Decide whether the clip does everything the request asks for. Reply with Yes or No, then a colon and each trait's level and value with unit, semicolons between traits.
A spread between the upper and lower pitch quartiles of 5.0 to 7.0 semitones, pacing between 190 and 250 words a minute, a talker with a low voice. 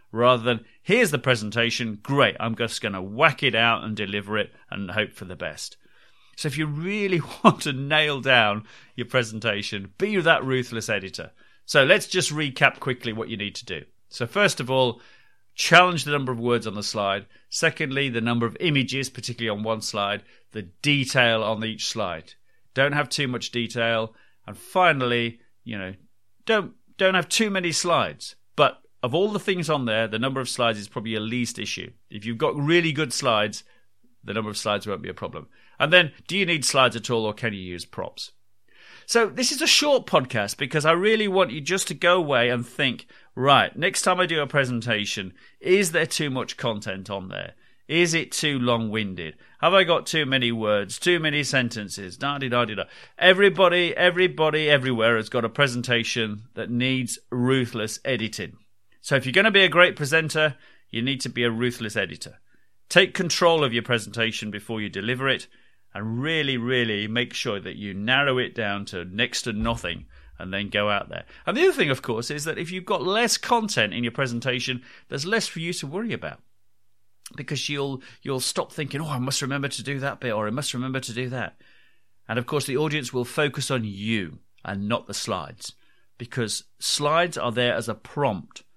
Yes: wide, 5.5 semitones; average, 195 wpm; low, 125 Hz